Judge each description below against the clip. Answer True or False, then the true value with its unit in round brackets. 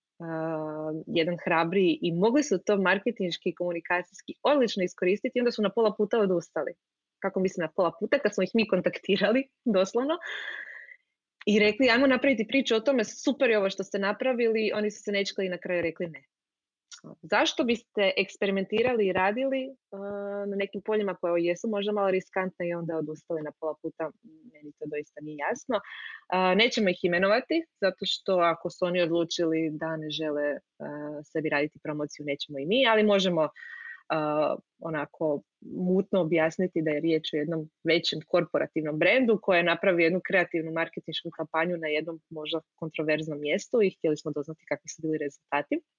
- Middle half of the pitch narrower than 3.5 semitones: False (4.6 semitones)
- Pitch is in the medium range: True (180 Hz)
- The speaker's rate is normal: False (170 wpm)